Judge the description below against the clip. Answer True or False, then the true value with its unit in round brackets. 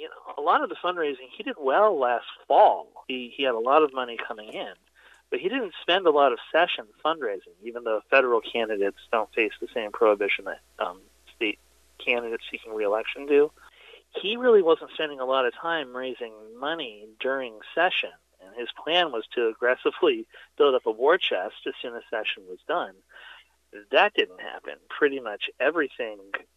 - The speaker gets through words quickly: False (185 wpm)